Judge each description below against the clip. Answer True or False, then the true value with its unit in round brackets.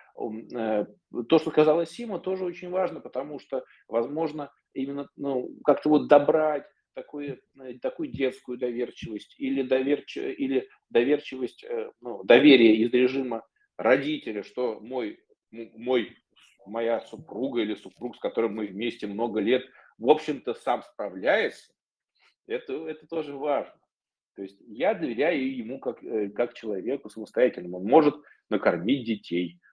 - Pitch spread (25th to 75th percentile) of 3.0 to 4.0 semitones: False (5.3 semitones)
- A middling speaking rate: True (125 wpm)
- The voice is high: False (135 Hz)